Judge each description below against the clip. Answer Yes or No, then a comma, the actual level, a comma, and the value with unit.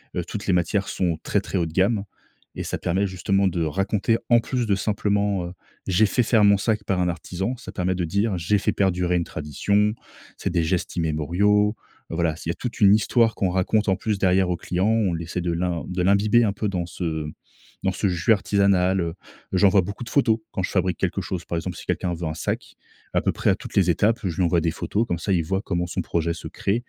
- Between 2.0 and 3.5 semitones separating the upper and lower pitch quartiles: Yes, average, 2.9 semitones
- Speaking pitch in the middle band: No, very low, 95 Hz